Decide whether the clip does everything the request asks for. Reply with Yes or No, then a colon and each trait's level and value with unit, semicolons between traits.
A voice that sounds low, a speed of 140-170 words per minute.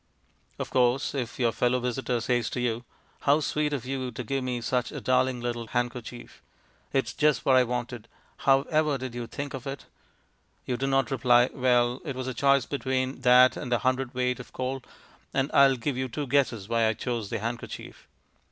No: low, 125 Hz; average, 195 wpm